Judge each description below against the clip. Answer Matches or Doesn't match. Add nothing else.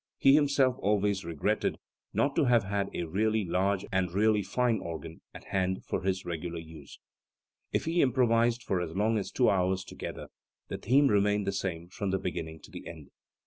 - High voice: Doesn't match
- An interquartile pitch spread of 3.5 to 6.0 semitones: Matches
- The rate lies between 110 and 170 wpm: Doesn't match